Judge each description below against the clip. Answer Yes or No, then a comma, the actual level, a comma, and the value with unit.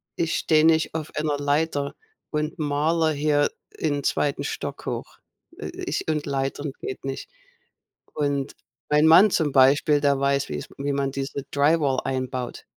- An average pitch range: No, narrow, 1.8 semitones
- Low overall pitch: No, medium, 145 Hz